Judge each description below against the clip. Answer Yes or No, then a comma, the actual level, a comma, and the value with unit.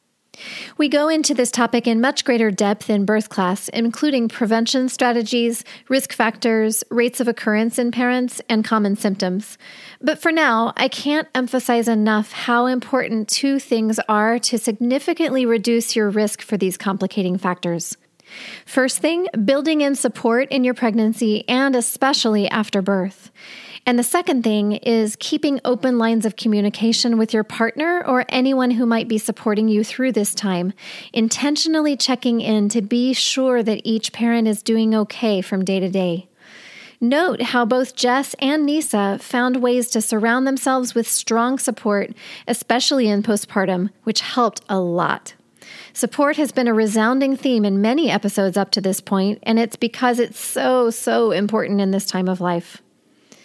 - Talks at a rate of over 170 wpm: No, average, 160 wpm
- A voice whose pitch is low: No, high, 230 Hz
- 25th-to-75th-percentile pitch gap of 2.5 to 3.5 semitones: Yes, average, 3.2 semitones